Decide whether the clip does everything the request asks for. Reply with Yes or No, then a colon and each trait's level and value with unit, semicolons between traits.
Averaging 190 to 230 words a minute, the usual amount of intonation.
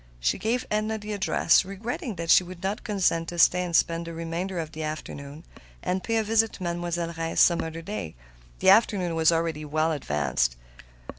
Yes: average, 195 wpm; average, 3.3 semitones